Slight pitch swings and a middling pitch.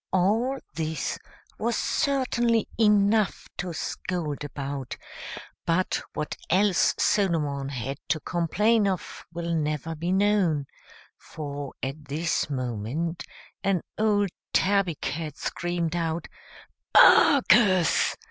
No: average, 5.1 semitones; medium, 170 Hz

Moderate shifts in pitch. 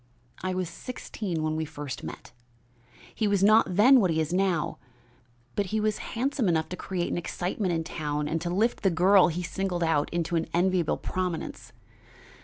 Yes: average, 3.4 semitones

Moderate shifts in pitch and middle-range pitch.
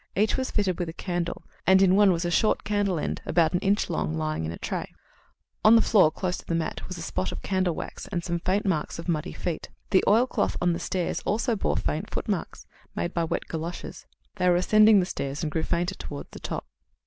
Yes: average, 3.0 semitones; medium, 180 Hz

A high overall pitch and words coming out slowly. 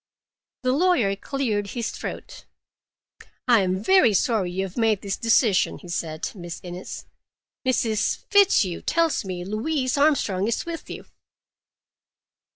Yes: high, 215 Hz; slow, 130 wpm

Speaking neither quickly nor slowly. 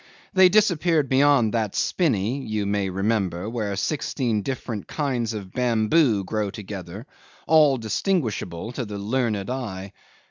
No: slow, 130 wpm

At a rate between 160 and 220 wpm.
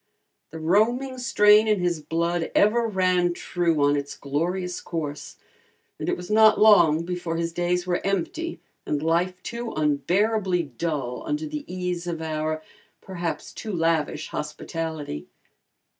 No: average, 140 wpm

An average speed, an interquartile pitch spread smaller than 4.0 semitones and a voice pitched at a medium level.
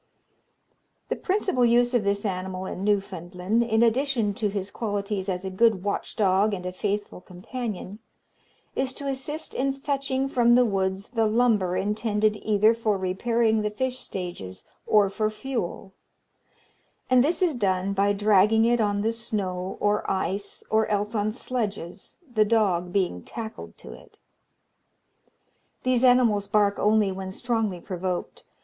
No: average, 150 wpm; average, 3.4 semitones; high, 210 Hz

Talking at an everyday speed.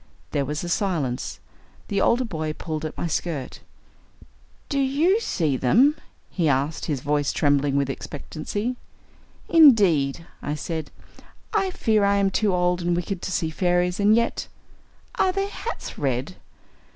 Yes: average, 150 wpm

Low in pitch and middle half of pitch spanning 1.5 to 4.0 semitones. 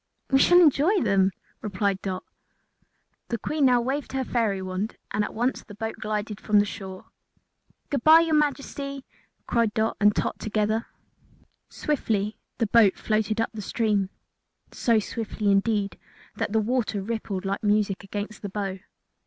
No: high, 215 Hz; average, 3.0 semitones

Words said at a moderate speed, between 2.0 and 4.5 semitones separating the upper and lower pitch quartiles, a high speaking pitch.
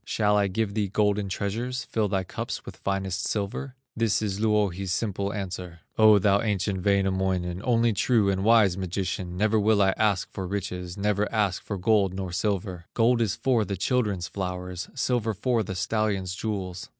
No: average, 175 wpm; narrow, 2.5 semitones; low, 100 Hz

